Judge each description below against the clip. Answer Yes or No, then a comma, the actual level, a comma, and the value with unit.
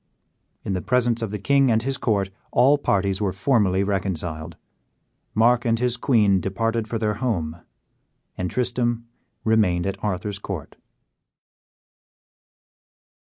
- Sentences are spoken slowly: Yes, slow, 125 wpm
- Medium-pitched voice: No, low, 105 Hz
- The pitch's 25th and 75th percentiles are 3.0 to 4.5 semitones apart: Yes, average, 3.8 semitones